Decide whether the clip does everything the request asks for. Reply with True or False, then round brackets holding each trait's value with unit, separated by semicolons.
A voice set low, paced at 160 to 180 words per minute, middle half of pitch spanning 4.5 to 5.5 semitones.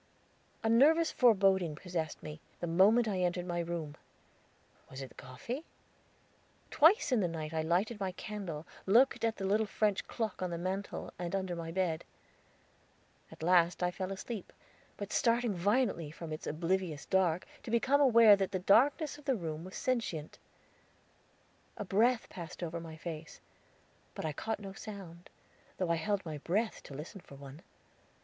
False (185 Hz; 170 wpm; 4.8 semitones)